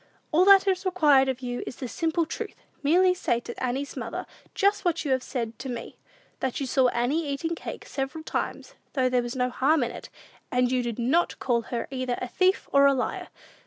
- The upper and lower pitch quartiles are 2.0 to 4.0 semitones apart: No, average, 4.8 semitones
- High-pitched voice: Yes, very high, 270 Hz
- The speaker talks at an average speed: No, fast, 215 wpm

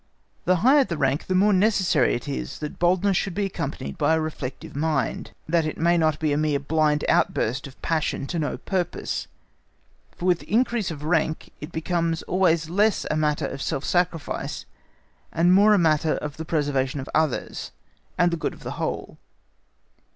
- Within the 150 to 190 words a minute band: Yes, average, 180 wpm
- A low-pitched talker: No, medium, 160 Hz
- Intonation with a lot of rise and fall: No, average, 3.2 semitones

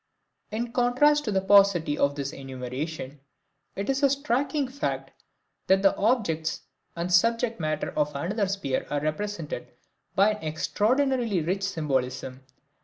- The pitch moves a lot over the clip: Yes, wide, 7.4 semitones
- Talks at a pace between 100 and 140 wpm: Yes, slow, 135 wpm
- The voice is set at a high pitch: Yes, high, 195 Hz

